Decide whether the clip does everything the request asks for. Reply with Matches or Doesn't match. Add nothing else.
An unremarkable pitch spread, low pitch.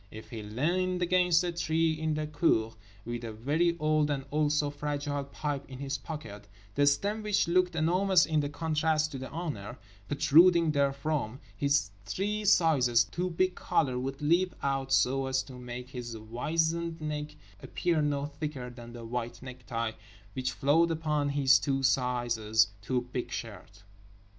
Doesn't match